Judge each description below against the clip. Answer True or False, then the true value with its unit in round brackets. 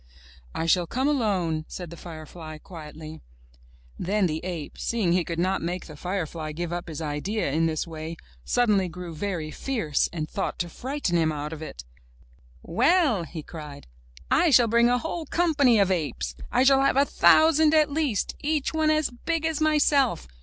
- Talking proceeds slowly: False (180 wpm)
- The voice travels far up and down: True (9.0 semitones)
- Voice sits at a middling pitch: True (180 Hz)